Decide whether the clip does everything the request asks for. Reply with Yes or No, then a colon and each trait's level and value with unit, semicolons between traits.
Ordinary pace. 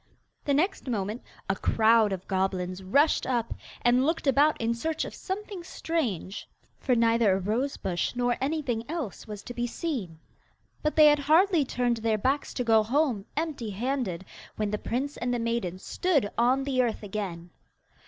Yes: average, 175 wpm